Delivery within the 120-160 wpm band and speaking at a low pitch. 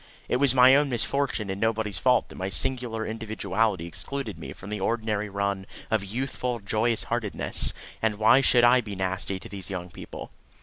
No: average, 180 wpm; low, 110 Hz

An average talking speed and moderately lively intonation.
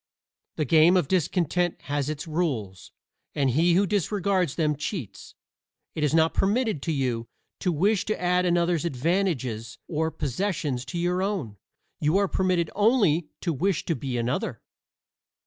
Yes: average, 150 wpm; average, 4.5 semitones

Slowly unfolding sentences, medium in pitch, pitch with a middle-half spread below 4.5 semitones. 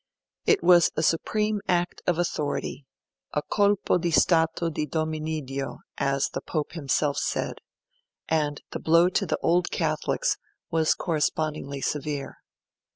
Yes: slow, 130 wpm; medium, 160 Hz; average, 2.8 semitones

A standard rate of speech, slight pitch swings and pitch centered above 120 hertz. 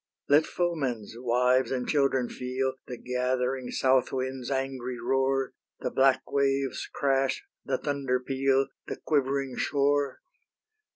No: slow, 120 wpm; narrow, 1.3 semitones; low, 135 Hz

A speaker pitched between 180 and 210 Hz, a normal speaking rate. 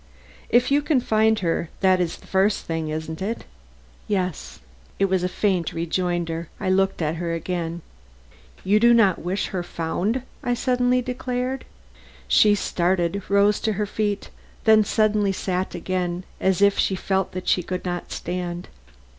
Yes: high, 190 Hz; average, 160 wpm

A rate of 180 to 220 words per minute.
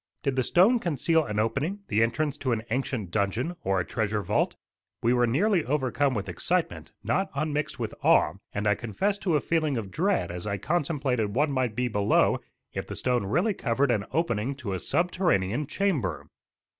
Yes: average, 185 wpm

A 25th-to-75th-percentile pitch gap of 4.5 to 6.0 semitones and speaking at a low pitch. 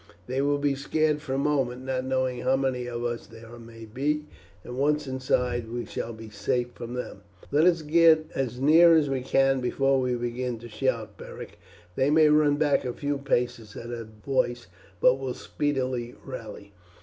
No: average, 3.1 semitones; low, 130 Hz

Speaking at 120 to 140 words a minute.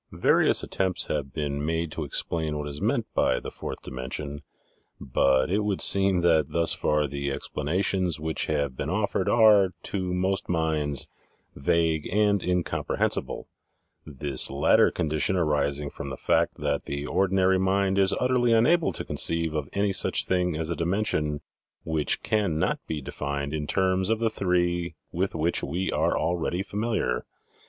No: average, 160 wpm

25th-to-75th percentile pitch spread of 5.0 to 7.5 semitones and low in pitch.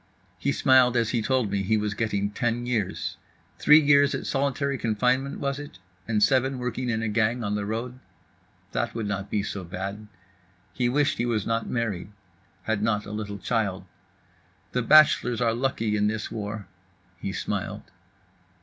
No: average, 3.3 semitones; low, 115 Hz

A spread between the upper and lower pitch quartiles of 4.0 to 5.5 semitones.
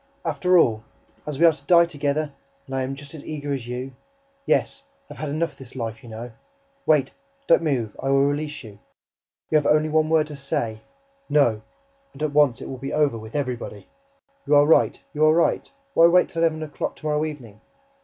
No: average, 3.3 semitones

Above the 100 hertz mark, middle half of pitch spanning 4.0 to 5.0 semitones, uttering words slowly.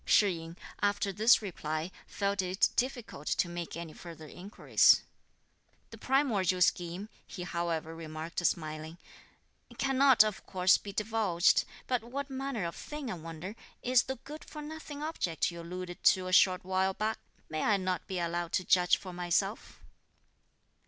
No: medium, 185 Hz; average, 4.5 semitones; average, 155 wpm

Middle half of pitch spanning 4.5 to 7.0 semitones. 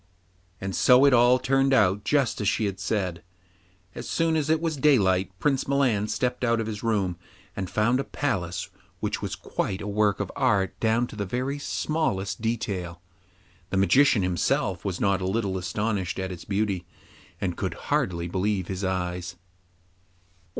Yes: average, 5.0 semitones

